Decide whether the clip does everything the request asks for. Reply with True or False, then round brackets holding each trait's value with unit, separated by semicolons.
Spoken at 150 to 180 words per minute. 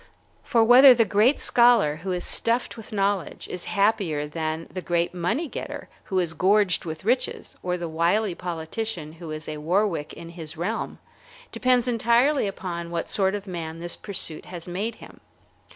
True (175 wpm)